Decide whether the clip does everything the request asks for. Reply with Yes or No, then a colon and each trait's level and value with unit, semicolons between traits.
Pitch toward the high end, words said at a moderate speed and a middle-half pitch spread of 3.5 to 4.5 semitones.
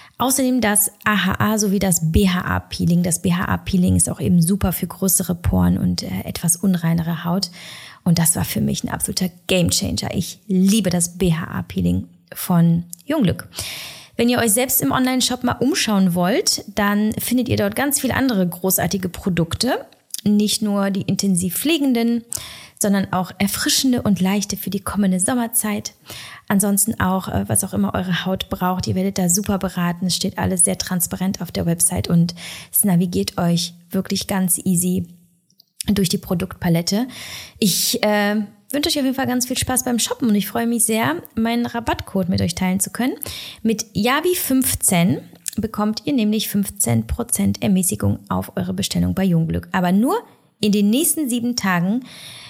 Yes: high, 195 Hz; average, 160 wpm; average, 3.9 semitones